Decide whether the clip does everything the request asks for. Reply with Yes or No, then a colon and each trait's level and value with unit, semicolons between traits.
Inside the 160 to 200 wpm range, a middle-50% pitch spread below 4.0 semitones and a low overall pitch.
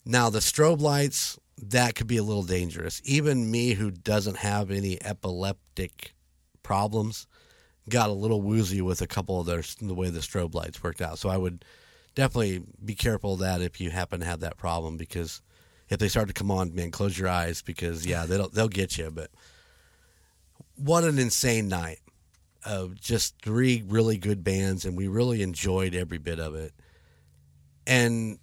No: average, 180 wpm; average, 4.3 semitones; very low, 95 Hz